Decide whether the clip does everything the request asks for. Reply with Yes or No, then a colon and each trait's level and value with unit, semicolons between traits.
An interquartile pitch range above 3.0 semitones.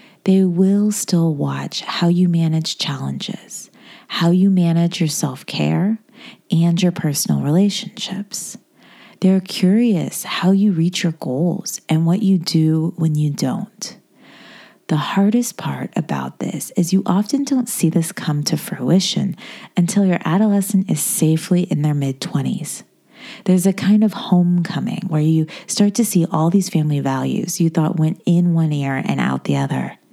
Yes: average, 4.0 semitones